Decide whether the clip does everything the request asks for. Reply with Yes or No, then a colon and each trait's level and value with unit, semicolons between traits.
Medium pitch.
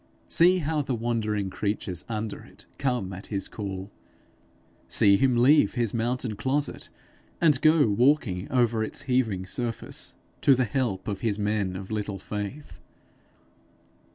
No: low, 115 Hz